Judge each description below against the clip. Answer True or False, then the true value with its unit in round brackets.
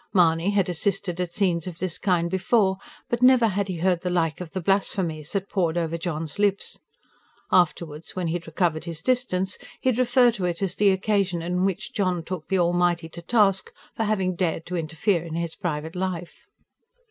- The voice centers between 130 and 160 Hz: False (180 Hz)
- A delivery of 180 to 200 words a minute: True (195 wpm)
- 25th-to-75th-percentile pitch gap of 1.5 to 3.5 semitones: True (2.7 semitones)